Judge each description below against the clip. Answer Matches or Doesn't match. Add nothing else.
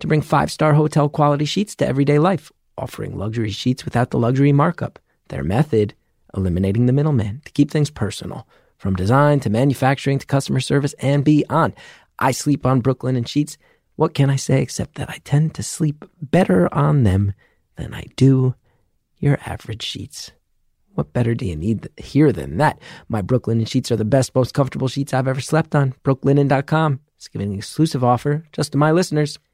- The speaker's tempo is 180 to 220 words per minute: Matches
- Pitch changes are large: Doesn't match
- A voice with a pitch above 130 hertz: Matches